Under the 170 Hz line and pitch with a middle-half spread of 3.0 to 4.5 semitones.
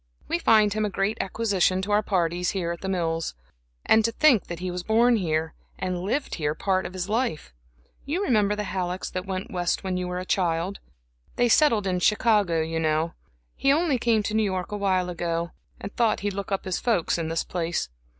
No: high, 190 Hz; average, 3.5 semitones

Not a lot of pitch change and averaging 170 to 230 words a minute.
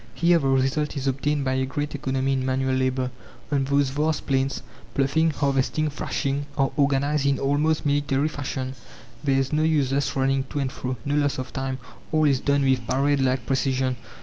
Yes: narrow, 1.6 semitones; average, 185 wpm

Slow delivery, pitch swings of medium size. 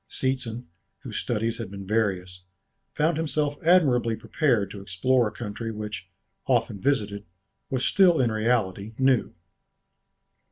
Yes: slow, 125 wpm; average, 4.4 semitones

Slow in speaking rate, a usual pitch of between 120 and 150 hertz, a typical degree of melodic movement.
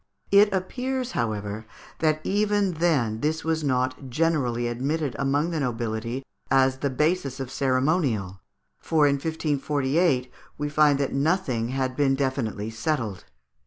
Yes: slow, 130 wpm; medium, 140 Hz; average, 4.2 semitones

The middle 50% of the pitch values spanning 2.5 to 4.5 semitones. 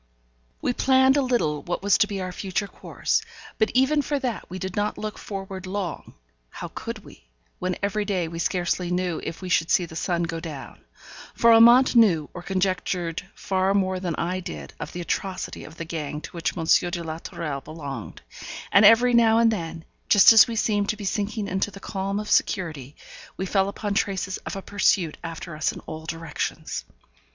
Yes: average, 3.8 semitones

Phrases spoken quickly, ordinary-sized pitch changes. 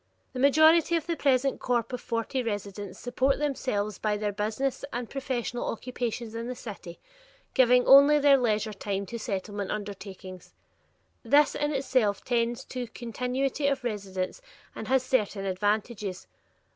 No: average, 145 wpm; average, 4.3 semitones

